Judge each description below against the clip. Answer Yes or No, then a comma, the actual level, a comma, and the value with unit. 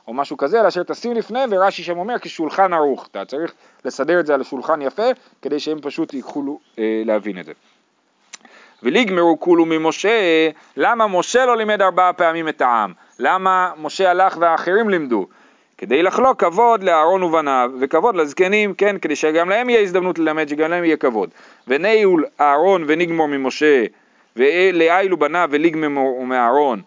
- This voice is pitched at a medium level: Yes, medium, 170 Hz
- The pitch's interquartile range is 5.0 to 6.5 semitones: No, average, 4.3 semitones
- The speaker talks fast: Yes, fast, 155 wpm